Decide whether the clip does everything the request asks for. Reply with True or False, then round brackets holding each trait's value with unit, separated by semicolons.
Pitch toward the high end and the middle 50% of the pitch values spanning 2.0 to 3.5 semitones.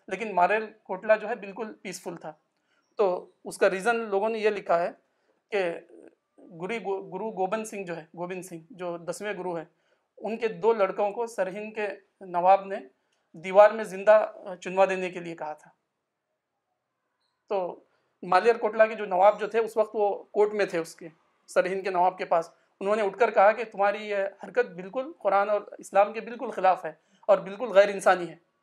True (195 Hz; 2.8 semitones)